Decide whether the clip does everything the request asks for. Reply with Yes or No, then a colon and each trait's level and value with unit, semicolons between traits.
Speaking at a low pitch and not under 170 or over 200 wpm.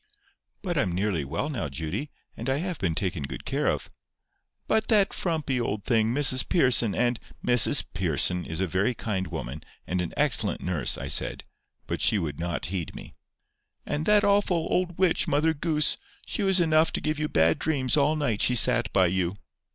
Yes: low, 120 Hz; average, 190 wpm